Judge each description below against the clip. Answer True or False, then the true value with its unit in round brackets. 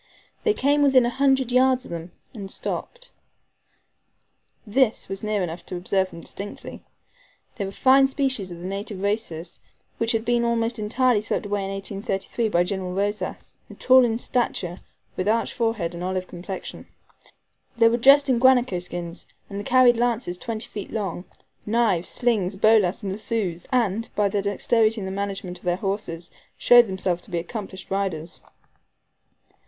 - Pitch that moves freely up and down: False (4.1 semitones)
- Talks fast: False (160 wpm)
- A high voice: True (205 Hz)